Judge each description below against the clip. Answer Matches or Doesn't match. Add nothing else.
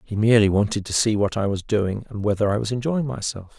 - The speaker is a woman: Doesn't match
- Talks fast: Matches